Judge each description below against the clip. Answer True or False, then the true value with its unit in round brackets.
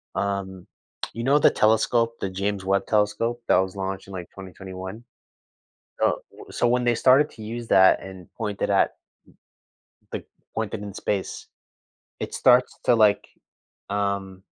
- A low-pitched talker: True (100 Hz)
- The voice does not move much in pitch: False (3.3 semitones)